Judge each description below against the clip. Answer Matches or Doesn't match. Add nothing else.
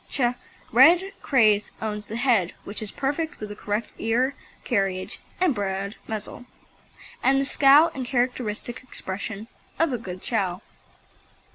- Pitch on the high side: Matches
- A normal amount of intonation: Matches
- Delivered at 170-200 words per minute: Doesn't match